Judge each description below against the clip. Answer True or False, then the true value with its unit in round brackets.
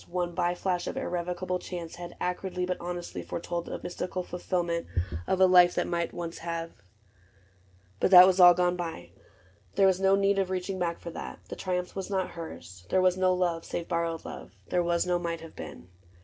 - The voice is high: False (180 Hz)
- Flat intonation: True (1.3 semitones)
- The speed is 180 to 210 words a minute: True (200 wpm)